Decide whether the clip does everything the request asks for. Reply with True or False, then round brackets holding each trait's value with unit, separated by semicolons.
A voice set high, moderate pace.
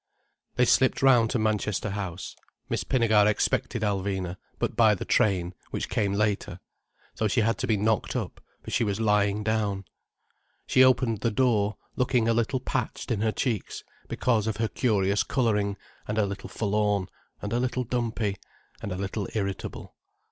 False (105 Hz; 170 wpm)